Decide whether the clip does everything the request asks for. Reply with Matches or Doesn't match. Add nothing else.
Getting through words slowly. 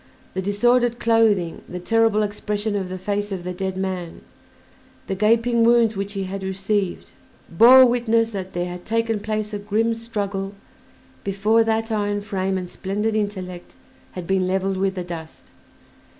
Doesn't match